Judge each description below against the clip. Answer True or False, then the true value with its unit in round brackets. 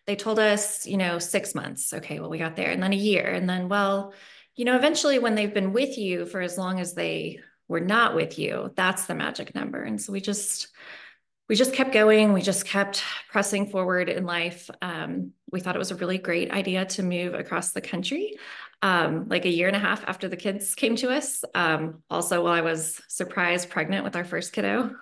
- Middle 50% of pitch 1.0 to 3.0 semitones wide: True (2.7 semitones)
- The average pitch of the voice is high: True (195 Hz)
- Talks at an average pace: False (225 wpm)